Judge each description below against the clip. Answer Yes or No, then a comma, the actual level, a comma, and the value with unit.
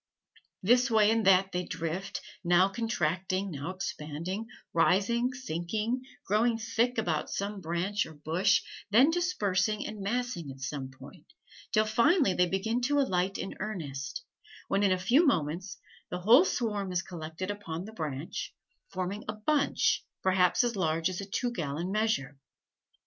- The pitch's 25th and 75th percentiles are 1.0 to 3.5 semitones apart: No, average, 4.5 semitones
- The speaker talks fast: No, average, 155 wpm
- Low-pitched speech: No, high, 195 Hz